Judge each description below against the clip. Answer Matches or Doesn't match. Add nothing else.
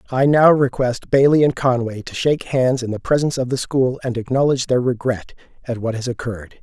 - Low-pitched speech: Matches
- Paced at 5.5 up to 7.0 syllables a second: Matches